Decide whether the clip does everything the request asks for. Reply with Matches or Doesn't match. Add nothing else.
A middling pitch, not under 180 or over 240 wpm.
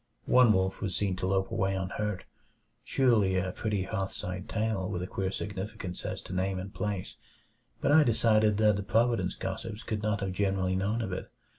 Doesn't match